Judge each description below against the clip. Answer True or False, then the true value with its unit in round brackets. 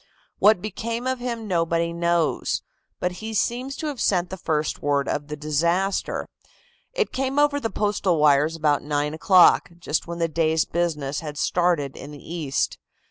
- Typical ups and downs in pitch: False (6.0 semitones)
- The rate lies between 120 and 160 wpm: False (170 wpm)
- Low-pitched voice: False (170 Hz)